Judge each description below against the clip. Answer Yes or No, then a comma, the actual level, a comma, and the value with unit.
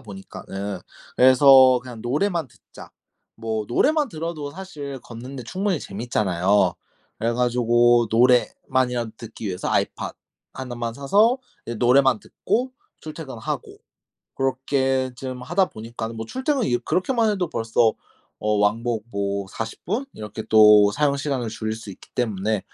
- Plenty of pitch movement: No, average, 4.4 semitones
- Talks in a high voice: No, low, 125 Hz